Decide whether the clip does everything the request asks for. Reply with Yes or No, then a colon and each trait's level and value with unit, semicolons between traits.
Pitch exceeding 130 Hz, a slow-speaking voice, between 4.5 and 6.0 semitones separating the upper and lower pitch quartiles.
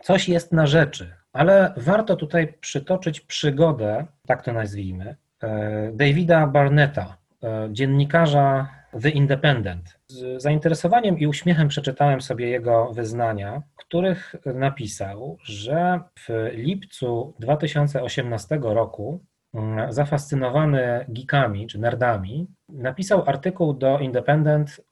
Yes: medium, 140 Hz; slow, 100 wpm; average, 5.3 semitones